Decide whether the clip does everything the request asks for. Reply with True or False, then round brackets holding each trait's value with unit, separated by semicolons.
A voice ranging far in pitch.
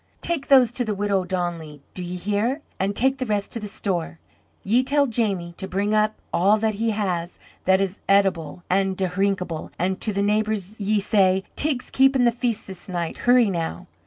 False (3.3 semitones)